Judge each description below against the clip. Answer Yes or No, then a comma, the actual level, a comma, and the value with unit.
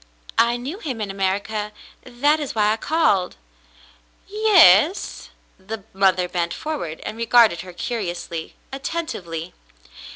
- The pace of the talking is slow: Yes, slow, 120 wpm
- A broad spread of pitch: Yes, wide, 7.4 semitones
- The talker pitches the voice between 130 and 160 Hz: No, high, 220 Hz